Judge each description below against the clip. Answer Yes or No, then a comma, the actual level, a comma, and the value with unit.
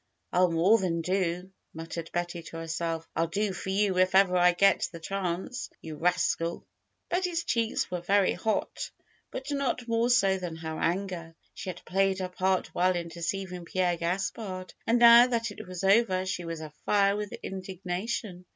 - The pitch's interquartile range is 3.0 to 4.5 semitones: No, narrow, 2.6 semitones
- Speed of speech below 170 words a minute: No, average, 180 wpm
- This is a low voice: No, medium, 185 Hz